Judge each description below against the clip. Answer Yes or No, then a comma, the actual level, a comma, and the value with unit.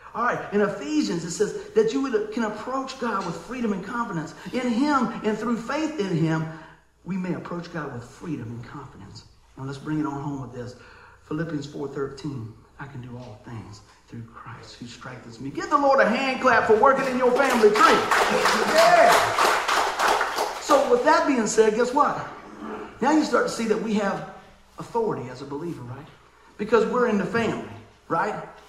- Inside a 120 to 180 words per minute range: No, average, 190 wpm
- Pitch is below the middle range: No, high, 195 Hz